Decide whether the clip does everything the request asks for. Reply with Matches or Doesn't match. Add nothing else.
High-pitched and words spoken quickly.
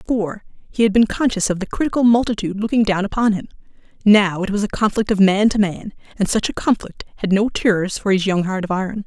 Matches